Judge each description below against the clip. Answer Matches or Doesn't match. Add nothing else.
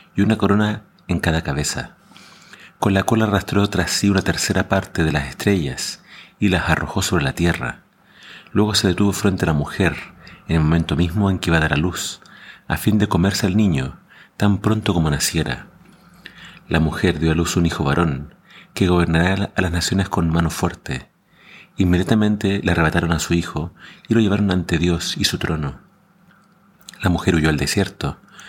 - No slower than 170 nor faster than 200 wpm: Matches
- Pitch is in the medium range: Doesn't match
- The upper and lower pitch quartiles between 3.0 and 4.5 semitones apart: Matches